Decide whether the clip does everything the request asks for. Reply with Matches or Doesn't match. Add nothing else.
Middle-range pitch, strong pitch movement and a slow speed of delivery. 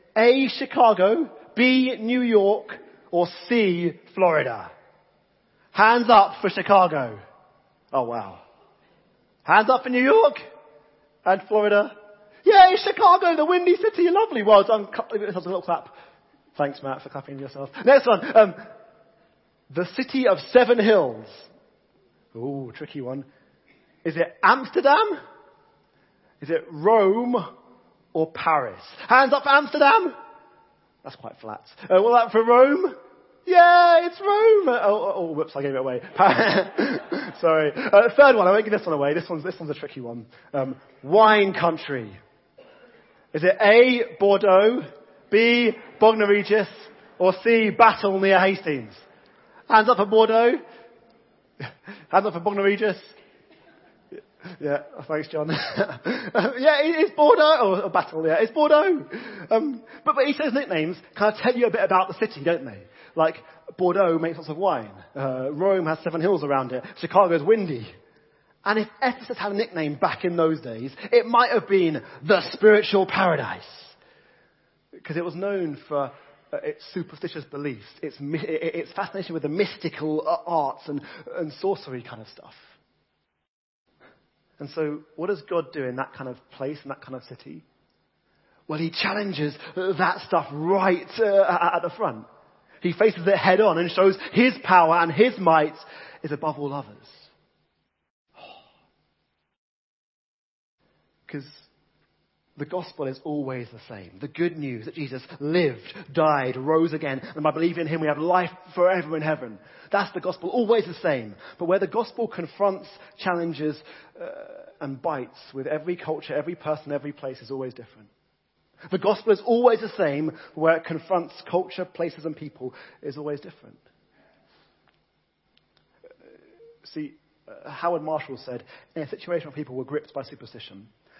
Doesn't match